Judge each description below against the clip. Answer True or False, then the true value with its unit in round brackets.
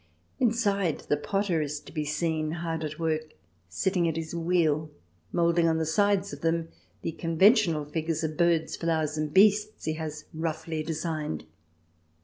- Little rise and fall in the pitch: True (1.8 semitones)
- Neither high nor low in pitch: True (165 Hz)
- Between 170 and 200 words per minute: False (160 wpm)